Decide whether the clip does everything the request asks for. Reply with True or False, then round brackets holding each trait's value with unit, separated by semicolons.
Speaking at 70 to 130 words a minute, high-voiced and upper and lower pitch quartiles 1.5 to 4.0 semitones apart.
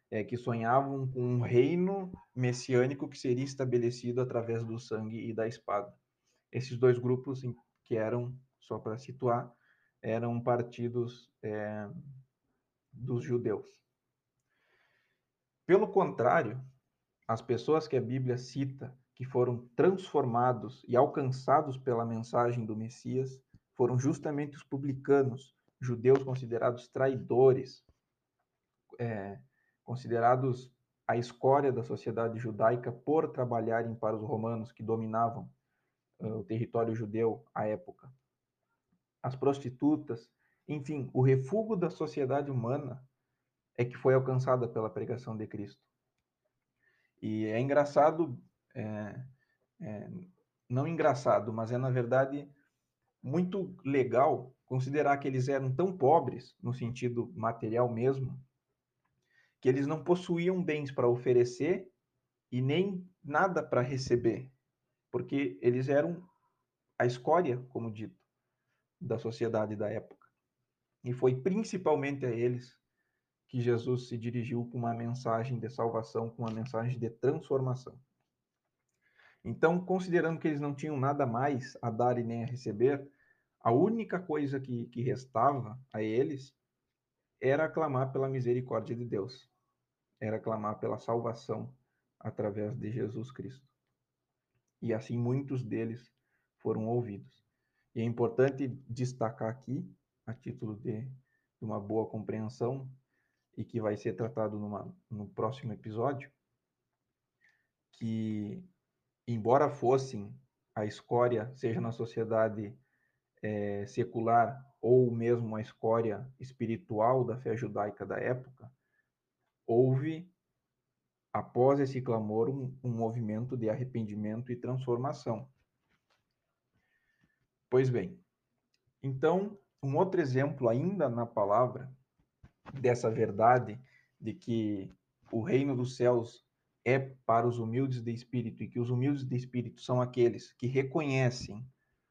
False (120 wpm; 125 Hz; 2.7 semitones)